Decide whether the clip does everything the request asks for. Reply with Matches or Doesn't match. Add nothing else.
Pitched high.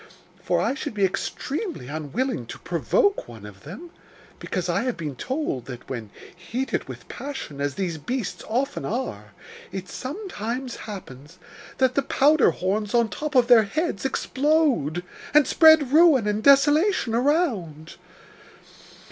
Matches